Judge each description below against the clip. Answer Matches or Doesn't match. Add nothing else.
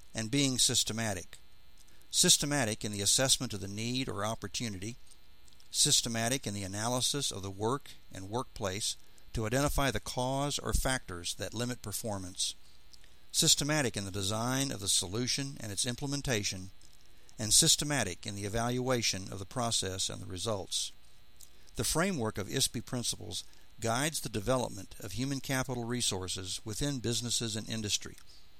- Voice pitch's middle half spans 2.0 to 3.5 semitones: Doesn't match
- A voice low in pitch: Matches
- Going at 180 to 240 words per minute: Doesn't match